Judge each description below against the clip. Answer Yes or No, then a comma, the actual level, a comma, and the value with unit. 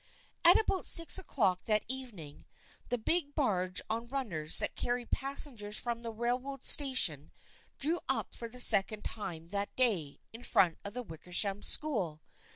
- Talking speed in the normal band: Yes, average, 160 wpm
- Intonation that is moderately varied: No, wide, 5.7 semitones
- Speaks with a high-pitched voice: Yes, high, 230 Hz